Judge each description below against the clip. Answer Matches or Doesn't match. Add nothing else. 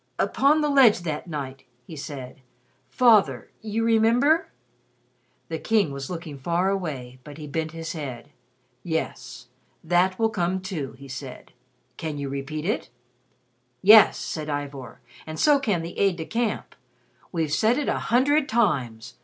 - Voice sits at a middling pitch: Matches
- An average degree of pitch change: Doesn't match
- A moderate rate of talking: Matches